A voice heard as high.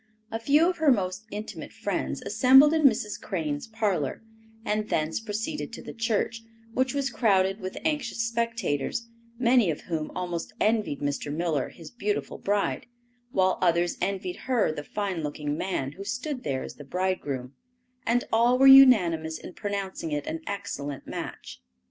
Yes: high, 200 Hz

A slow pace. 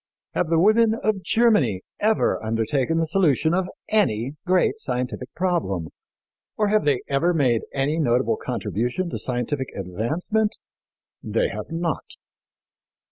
Yes: slow, 130 wpm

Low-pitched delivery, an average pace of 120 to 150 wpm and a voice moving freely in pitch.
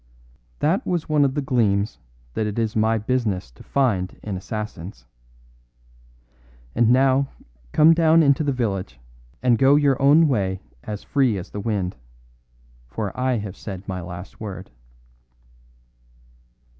Yes: low, 110 Hz; average, 140 wpm; wide, 5.8 semitones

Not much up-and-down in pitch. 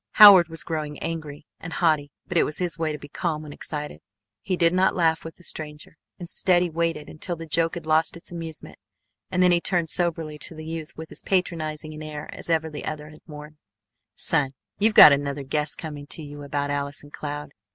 Yes: narrow, 2.2 semitones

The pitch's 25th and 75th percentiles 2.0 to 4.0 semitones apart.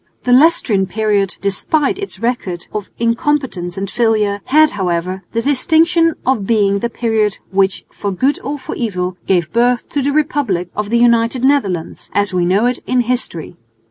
No: average, 5.1 semitones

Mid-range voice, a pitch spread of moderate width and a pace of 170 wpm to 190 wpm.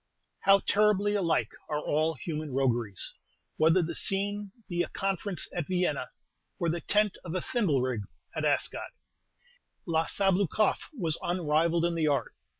No: medium, 170 Hz; average, 4.1 semitones; average, 145 wpm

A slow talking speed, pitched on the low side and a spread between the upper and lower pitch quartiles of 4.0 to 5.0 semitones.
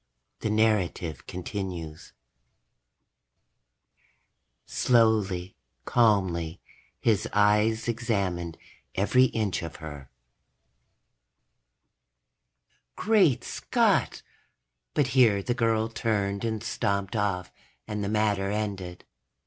No: slow, 80 wpm; low, 105 Hz; average, 3.4 semitones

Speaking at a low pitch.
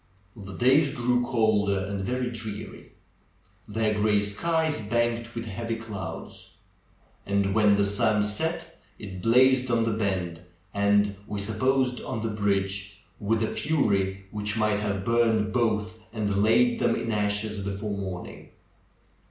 Yes: low, 105 Hz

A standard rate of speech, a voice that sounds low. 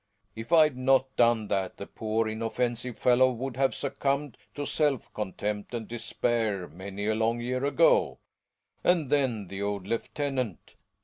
Yes: average, 145 wpm; low, 120 Hz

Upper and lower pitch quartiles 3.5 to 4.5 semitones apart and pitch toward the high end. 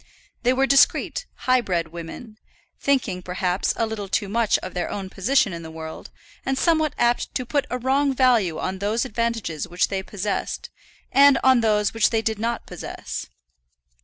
No: average, 5.3 semitones; high, 220 Hz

